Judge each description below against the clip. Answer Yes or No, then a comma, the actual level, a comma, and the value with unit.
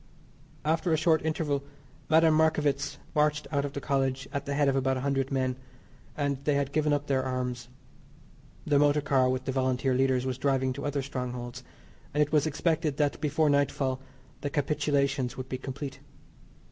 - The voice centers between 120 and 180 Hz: Yes, medium, 140 Hz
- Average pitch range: No, narrow, 2.3 semitones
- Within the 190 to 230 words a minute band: No, average, 175 wpm